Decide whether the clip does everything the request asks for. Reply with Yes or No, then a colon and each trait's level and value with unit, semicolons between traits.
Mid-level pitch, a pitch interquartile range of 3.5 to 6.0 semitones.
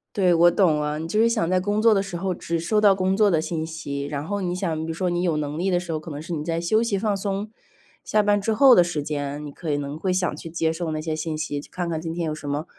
Yes: medium, 170 Hz; average, 3.8 semitones